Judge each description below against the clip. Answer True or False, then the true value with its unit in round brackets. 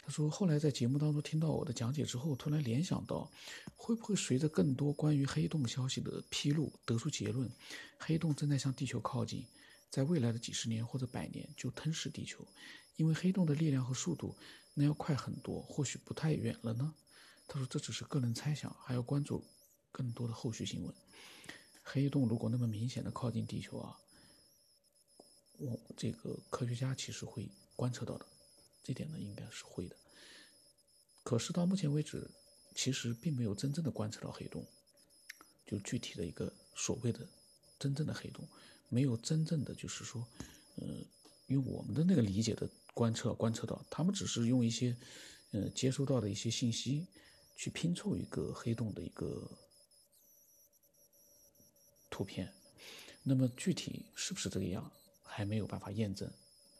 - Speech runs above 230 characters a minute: True (260 characters per minute)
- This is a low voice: True (130 Hz)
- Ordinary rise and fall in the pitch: True (4.3 semitones)